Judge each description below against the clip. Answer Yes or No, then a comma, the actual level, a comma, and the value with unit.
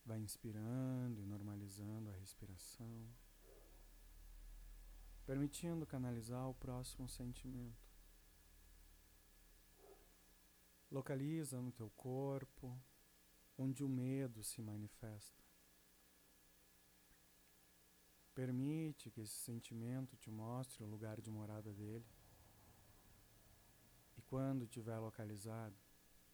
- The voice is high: No, low, 105 Hz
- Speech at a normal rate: No, slow, 80 wpm